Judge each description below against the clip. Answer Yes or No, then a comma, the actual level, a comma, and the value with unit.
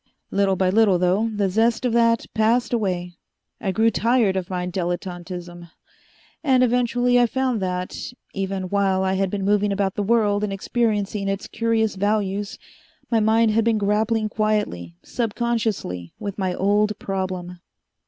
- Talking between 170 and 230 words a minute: No, average, 155 wpm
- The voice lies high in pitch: Yes, high, 205 Hz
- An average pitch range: Yes, average, 3.1 semitones